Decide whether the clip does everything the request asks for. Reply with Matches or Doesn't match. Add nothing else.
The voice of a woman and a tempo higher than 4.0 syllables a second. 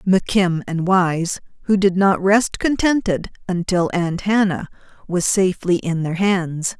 Matches